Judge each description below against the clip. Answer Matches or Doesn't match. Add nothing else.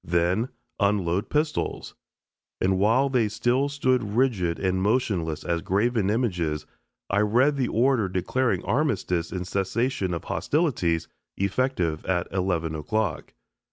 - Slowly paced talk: Matches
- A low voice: Matches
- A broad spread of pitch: Matches